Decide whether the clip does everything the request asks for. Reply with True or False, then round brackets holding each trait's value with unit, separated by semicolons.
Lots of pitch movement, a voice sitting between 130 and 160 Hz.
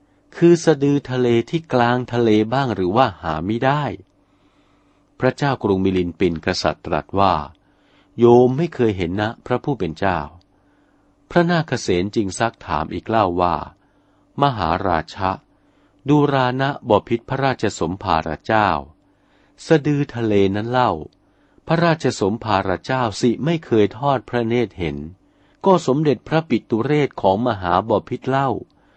False (5.8 semitones; 115 Hz)